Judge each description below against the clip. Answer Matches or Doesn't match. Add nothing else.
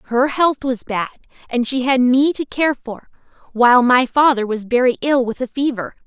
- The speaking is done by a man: Doesn't match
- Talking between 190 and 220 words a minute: Matches